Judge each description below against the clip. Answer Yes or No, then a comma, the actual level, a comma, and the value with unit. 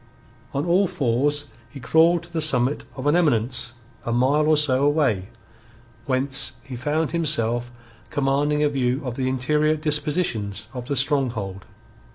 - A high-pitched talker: No, medium, 140 Hz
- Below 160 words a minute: Yes, average, 150 wpm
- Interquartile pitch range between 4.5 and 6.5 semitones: No, average, 3.5 semitones